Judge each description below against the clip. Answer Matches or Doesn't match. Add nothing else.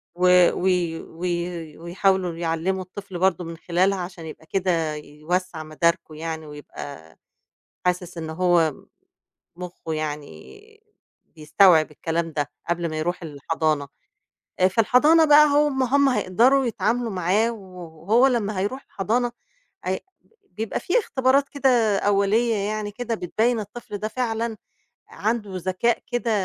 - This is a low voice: Doesn't match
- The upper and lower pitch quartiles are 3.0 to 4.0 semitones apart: Doesn't match